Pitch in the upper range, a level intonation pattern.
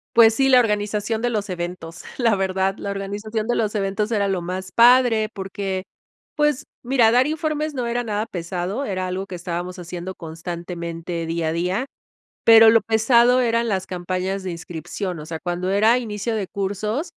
No: high, 200 Hz; average, 4.1 semitones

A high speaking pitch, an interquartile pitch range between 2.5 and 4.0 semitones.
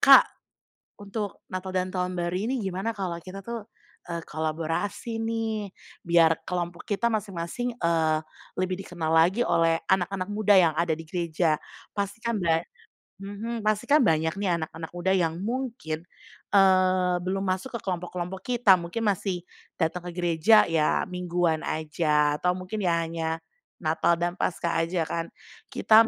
No: medium, 180 Hz; average, 3.4 semitones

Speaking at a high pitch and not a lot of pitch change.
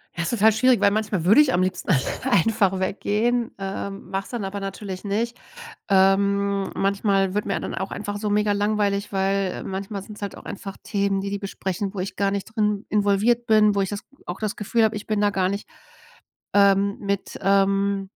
Yes: high, 200 Hz; narrow, 1.3 semitones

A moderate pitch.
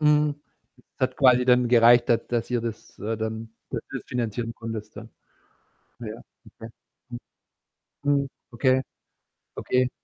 No: low, 120 Hz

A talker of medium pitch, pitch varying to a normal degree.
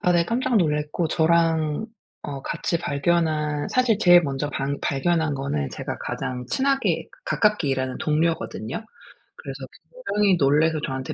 Yes: medium, 155 Hz; average, 3.7 semitones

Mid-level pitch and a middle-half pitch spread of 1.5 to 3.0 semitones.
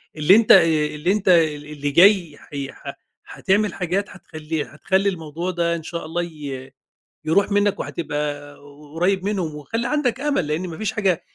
No: medium, 170 Hz; average, 4.5 semitones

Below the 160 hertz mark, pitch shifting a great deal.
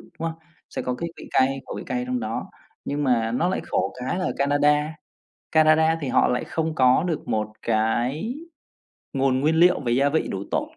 No: medium, 140 Hz; average, 4.3 semitones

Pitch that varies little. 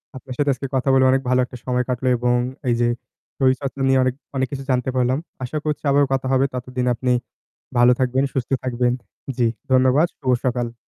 Yes: narrow, 1.2 semitones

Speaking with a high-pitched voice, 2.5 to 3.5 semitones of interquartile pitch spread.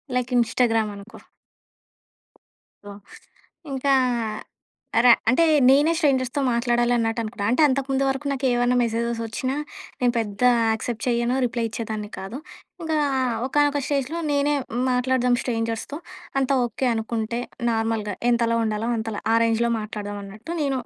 Yes: high, 240 Hz; average, 2.9 semitones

